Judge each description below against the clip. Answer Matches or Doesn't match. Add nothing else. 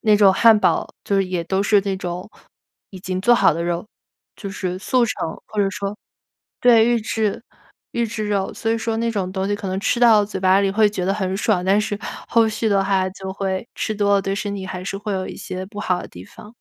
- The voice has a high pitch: Matches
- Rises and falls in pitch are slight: Matches